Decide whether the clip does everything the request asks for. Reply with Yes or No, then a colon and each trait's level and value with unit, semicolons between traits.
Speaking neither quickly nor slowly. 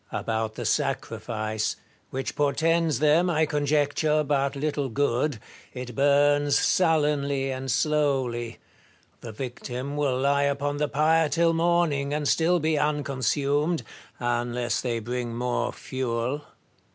No: slow, 125 wpm